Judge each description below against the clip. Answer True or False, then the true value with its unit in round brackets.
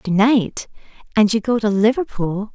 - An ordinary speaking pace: True (165 wpm)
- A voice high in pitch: True (215 Hz)